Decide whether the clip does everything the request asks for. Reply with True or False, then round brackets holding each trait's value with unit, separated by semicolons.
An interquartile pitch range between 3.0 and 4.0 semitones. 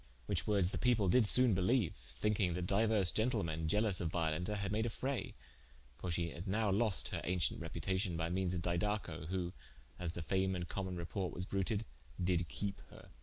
True (3.3 semitones)